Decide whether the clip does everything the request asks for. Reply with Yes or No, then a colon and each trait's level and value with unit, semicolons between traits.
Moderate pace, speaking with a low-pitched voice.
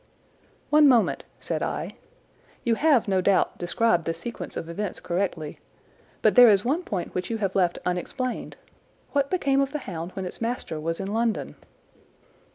No: average, 165 wpm; high, 205 Hz